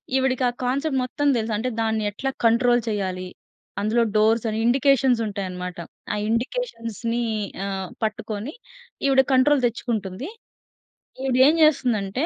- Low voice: No, high, 235 Hz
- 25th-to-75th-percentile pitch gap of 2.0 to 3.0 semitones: No, average, 3.7 semitones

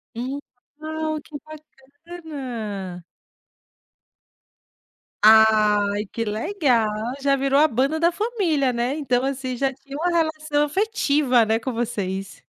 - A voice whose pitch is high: Yes, very high, 270 Hz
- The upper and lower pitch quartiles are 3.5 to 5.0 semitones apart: No, wide, 5.4 semitones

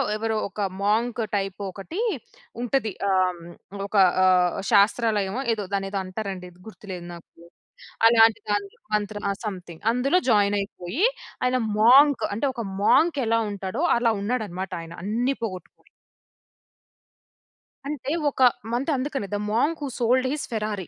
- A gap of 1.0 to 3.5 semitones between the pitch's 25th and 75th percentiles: No, average, 4.1 semitones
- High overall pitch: Yes, high, 215 Hz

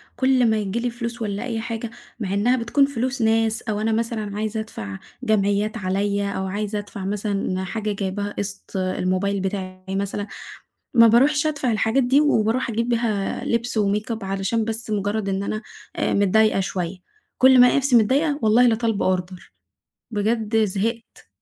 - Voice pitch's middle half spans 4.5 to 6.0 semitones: No, average, 2.7 semitones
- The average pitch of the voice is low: No, high, 215 Hz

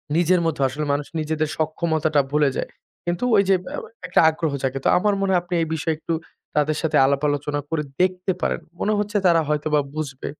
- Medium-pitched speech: Yes, medium, 155 Hz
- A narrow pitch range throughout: No, average, 3.0 semitones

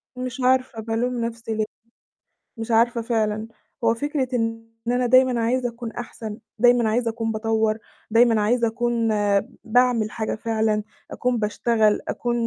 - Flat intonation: Yes, narrow, 1.7 semitones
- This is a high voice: Yes, high, 230 Hz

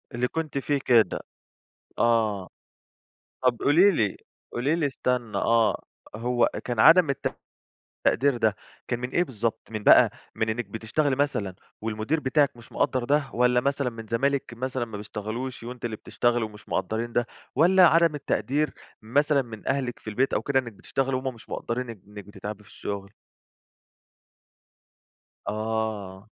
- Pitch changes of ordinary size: Yes, average, 4.0 semitones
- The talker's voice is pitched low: Yes, low, 120 Hz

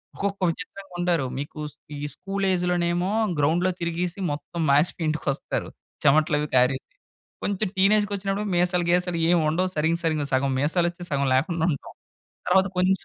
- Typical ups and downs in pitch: Yes, average, 3.5 semitones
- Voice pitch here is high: No, medium, 175 Hz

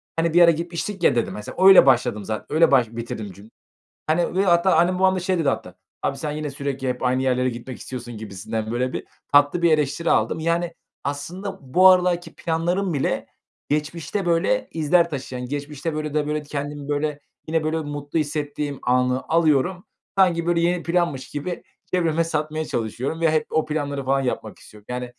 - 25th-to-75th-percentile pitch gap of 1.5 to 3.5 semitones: No, average, 4.3 semitones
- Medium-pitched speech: Yes, medium, 150 Hz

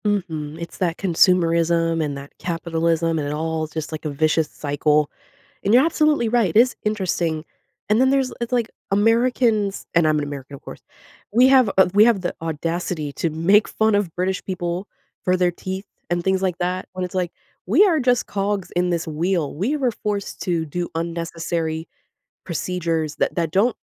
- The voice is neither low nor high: Yes, medium, 175 Hz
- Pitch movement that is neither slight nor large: Yes, average, 4.1 semitones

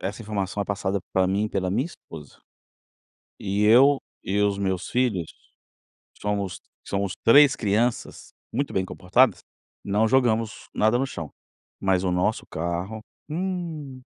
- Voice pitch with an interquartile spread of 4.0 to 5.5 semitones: Yes, average, 4.3 semitones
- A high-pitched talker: No, low, 105 Hz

